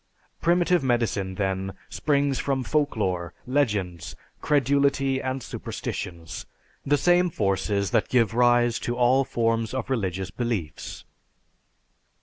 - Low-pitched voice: Yes, low, 120 Hz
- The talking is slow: Yes, slow, 110 wpm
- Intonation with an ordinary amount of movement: No, wide, 5.9 semitones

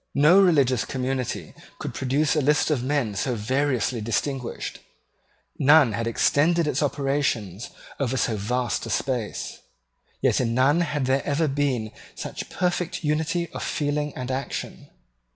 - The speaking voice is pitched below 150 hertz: Yes, low, 135 Hz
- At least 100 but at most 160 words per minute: Yes, average, 140 wpm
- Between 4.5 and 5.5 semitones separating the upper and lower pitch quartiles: No, average, 3.4 semitones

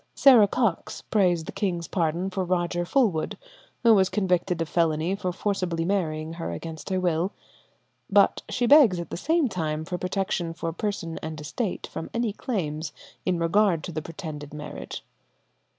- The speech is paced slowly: No, average, 165 wpm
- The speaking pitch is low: No, medium, 175 Hz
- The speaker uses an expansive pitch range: No, average, 3.4 semitones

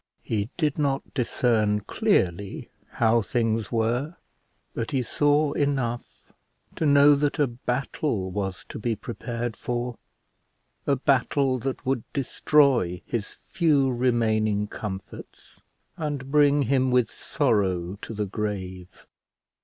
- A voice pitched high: No, low, 120 Hz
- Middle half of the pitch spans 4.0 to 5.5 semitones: Yes, average, 4.7 semitones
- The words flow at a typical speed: No, slow, 120 wpm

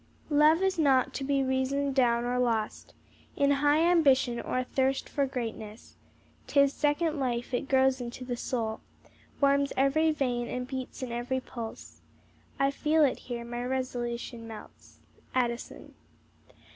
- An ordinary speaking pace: Yes, average, 145 wpm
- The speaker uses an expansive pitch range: No, narrow, 2.6 semitones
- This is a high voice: Yes, very high, 260 Hz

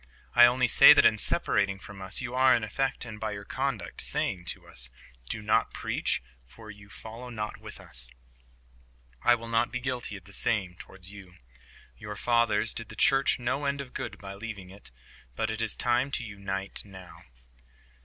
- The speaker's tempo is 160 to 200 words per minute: Yes, average, 190 wpm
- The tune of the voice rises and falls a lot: No, average, 3.7 semitones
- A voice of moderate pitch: No, low, 110 Hz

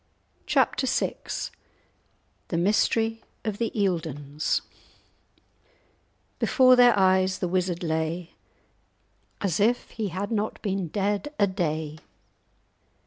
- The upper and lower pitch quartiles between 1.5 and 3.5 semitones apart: No, average, 4.2 semitones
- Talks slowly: Yes, slow, 100 wpm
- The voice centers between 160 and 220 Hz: Yes, high, 190 Hz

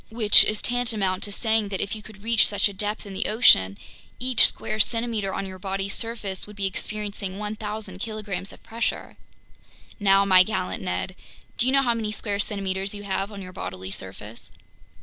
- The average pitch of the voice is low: No, high, 205 Hz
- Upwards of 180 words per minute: Yes, average, 190 wpm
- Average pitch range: No, narrow, 2.3 semitones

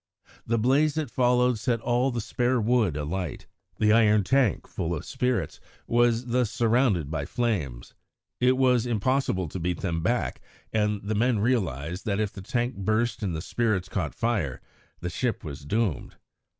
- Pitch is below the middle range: Yes, low, 110 Hz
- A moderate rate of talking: Yes, average, 165 wpm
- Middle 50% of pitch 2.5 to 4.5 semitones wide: No, average, 5.1 semitones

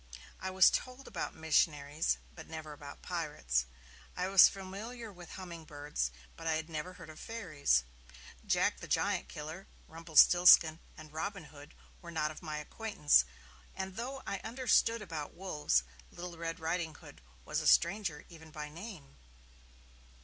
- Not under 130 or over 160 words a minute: Yes, average, 145 wpm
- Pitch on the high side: No, medium, 165 Hz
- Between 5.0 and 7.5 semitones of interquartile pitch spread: No, average, 3.8 semitones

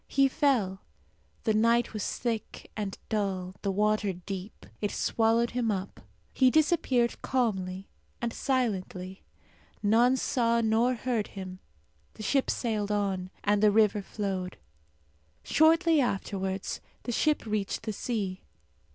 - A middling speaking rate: No, slow, 125 wpm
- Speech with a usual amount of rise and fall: Yes, average, 3.7 semitones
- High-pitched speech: Yes, high, 215 Hz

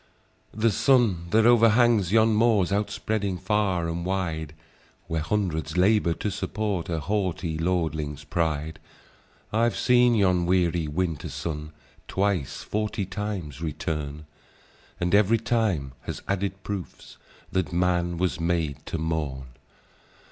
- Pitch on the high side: No, very low, 90 Hz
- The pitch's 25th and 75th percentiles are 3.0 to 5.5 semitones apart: Yes, average, 4.5 semitones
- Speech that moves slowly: Yes, slow, 125 wpm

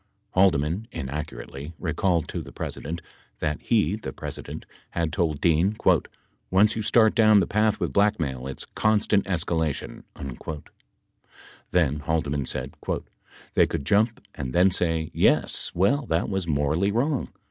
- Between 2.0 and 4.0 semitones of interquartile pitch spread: No, average, 5.3 semitones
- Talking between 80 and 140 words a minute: Yes, slow, 135 wpm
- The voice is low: Yes, very low, 85 Hz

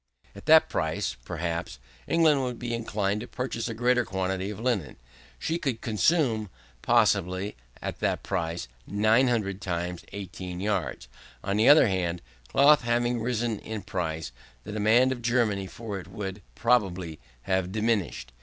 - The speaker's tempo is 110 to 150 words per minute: Yes, average, 145 wpm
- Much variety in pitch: No, average, 4.3 semitones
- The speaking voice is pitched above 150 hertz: No, low, 105 Hz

